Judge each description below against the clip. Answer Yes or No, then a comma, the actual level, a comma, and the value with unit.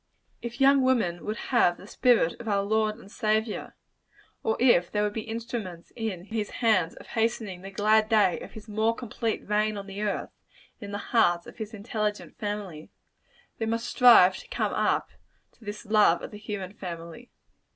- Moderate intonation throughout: No, narrow, 2.3 semitones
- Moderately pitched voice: No, high, 215 Hz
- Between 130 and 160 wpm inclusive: No, average, 185 wpm